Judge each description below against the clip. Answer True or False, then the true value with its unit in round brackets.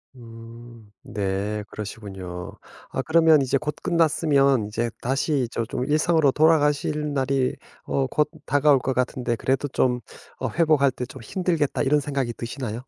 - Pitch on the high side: False (135 Hz)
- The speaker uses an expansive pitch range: False (4.2 semitones)